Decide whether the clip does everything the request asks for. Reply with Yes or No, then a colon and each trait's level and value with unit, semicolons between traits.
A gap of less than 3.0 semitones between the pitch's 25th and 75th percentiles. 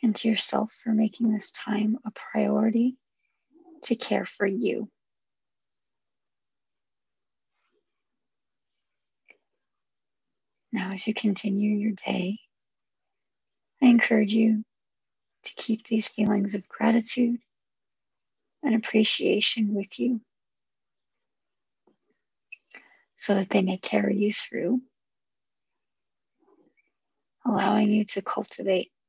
Yes: narrow, 2.6 semitones